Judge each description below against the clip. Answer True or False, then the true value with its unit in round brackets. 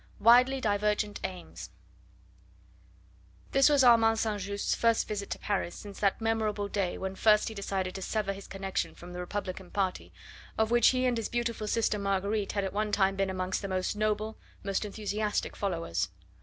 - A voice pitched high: True (205 Hz)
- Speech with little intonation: True (2.3 semitones)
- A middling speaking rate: True (175 wpm)